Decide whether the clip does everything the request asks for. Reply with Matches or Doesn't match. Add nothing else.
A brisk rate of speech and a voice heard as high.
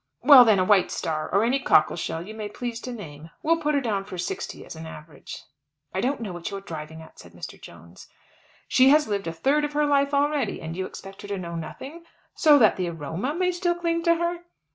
Matches